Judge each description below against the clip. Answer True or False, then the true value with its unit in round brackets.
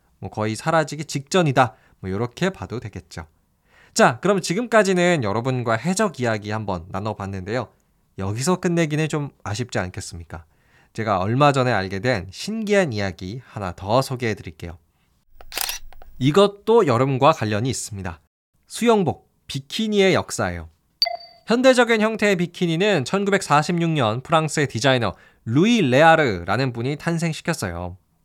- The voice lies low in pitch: True (130 Hz)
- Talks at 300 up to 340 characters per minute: True (310 characters per minute)